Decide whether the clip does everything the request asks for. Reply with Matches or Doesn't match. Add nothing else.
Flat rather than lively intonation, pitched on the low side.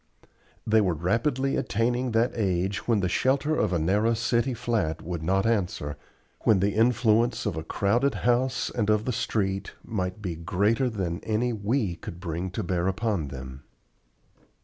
Doesn't match